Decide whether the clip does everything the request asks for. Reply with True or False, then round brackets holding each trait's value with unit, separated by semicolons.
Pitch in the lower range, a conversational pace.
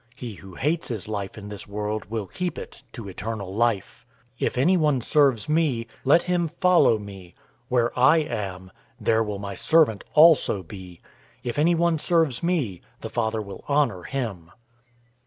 True (115 Hz; 160 wpm)